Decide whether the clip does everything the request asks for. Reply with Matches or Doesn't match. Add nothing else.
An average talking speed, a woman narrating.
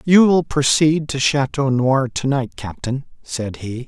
Doesn't match